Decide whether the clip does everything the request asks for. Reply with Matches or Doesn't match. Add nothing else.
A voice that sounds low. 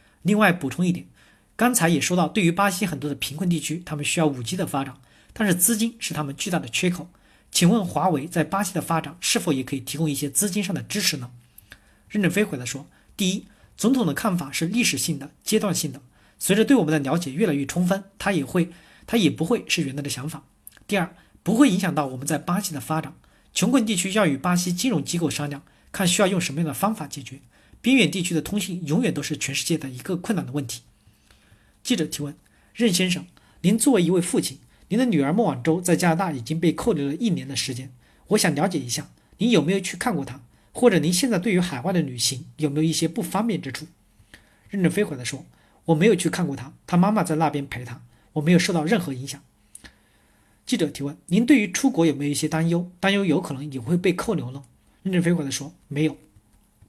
Doesn't match